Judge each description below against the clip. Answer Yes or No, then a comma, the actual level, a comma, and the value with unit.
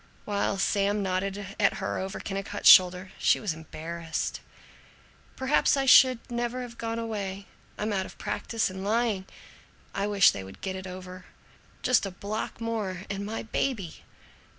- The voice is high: Yes, high, 200 Hz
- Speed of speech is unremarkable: Yes, average, 155 wpm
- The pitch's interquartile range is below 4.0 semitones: Yes, average, 3.3 semitones